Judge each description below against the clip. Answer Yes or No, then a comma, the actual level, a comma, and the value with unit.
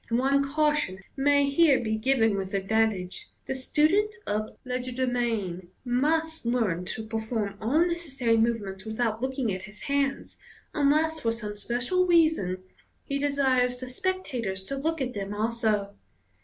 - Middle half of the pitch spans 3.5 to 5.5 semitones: Yes, average, 4.7 semitones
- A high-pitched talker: Yes, high, 245 Hz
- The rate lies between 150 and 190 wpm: No, average, 140 wpm